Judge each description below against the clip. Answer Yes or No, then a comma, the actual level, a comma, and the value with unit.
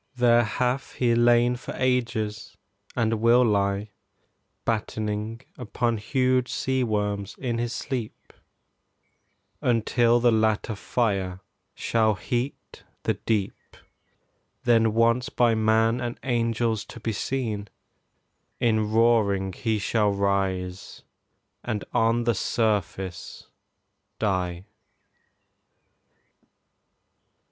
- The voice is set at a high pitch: No, low, 115 Hz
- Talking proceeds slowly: Yes, slow, 95 wpm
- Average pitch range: No, narrow, 2.3 semitones